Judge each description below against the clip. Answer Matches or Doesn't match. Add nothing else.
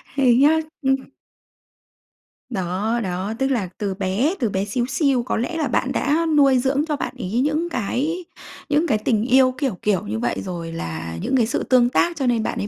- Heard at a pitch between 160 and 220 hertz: Doesn't match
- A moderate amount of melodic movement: Doesn't match